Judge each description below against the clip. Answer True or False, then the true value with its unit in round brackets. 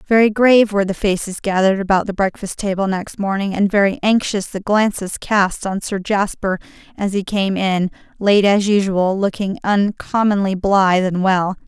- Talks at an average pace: True (170 wpm)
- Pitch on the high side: True (195 Hz)